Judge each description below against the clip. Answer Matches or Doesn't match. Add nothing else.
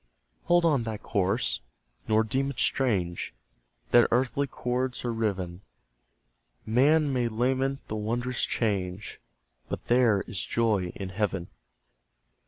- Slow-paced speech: Matches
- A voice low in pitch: Matches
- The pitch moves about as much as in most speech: Matches